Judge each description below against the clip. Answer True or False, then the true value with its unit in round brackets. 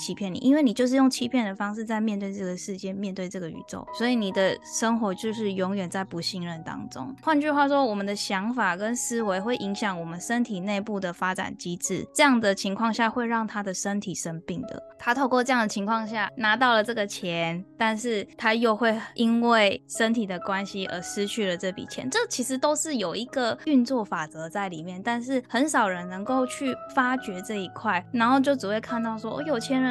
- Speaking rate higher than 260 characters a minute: True (320 characters per minute)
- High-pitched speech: True (220 Hz)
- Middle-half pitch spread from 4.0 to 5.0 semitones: True (4.5 semitones)